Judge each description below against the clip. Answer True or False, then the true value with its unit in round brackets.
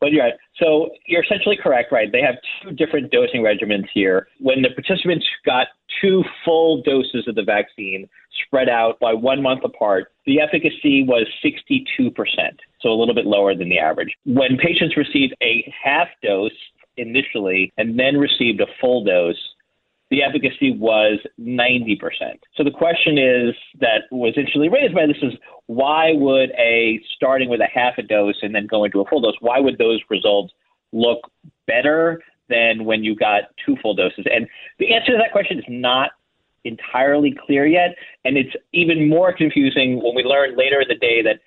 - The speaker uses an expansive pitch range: True (6.2 semitones)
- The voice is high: False (135 Hz)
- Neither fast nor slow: True (180 wpm)